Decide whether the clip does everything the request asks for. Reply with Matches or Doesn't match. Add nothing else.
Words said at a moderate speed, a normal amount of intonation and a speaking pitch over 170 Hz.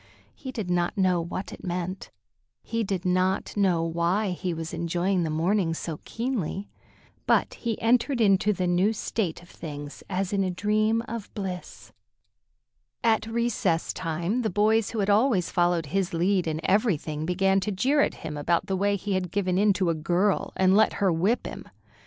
Matches